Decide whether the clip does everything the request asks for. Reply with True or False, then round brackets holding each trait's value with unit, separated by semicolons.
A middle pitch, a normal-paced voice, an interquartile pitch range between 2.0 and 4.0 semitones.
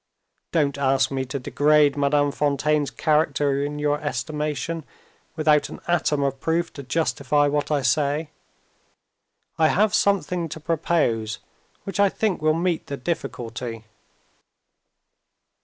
False (150 Hz; 125 wpm; 2.5 semitones)